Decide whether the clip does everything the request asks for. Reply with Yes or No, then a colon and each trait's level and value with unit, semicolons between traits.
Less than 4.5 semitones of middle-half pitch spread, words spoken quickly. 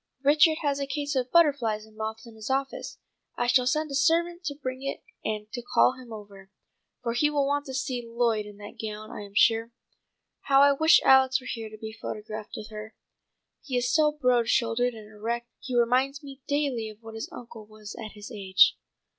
Yes: average, 4.1 semitones; fast, 210 wpm